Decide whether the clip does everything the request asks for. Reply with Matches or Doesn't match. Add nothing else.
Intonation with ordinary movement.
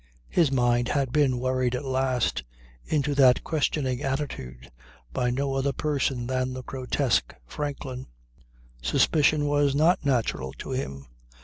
Doesn't match